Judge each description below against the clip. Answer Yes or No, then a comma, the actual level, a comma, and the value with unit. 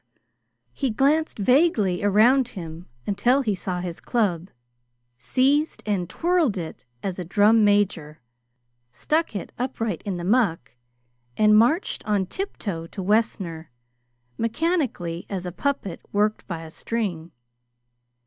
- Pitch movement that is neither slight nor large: No, wide, 5.8 semitones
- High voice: Yes, high, 205 Hz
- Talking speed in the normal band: No, slow, 125 wpm